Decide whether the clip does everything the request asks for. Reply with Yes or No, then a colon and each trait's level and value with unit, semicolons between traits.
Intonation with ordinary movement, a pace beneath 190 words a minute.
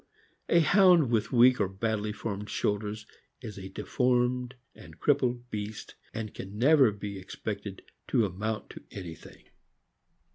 Yes: average, 3.4 semitones; slow, 135 wpm